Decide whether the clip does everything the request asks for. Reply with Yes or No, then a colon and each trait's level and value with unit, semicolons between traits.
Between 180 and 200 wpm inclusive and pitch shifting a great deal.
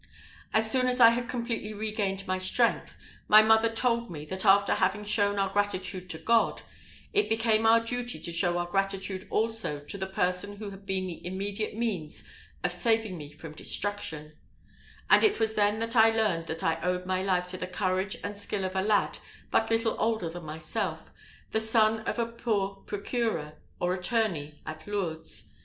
No: average, 185 wpm; average, 3.5 semitones